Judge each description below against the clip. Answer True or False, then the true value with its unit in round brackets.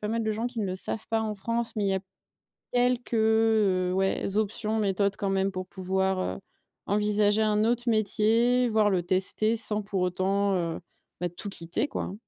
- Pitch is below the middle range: False (210 Hz)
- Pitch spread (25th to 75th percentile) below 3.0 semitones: True (2.5 semitones)